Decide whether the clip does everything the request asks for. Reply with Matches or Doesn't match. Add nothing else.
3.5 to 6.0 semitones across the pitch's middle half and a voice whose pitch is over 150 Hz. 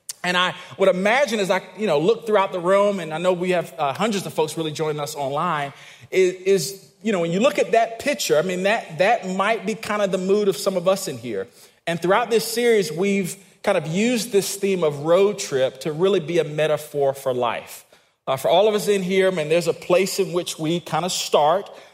Matches